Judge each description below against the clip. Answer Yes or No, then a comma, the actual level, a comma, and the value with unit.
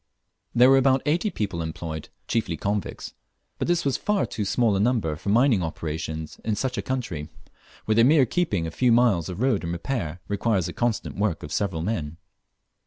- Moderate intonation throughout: No, wide, 7.2 semitones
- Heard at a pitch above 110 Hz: No, low, 105 Hz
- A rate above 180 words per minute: Yes, average, 190 wpm